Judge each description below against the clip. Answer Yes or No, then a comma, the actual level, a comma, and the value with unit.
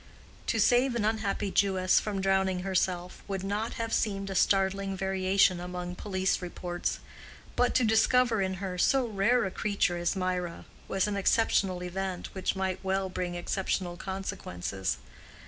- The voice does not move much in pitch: Yes, narrow, 1.8 semitones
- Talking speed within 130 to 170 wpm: Yes, average, 150 wpm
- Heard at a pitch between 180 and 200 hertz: Yes, high, 190 Hz